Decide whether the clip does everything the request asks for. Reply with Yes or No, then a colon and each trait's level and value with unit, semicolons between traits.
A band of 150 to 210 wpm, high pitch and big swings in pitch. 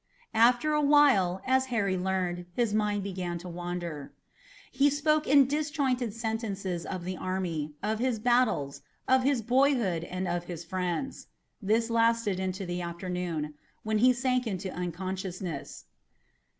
No: average, 140 wpm; high, 200 Hz; wide, 5.9 semitones